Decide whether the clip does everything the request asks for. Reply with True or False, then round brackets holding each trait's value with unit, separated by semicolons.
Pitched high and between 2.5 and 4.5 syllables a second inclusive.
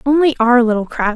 False (245 Hz; 5.8 syllables/s)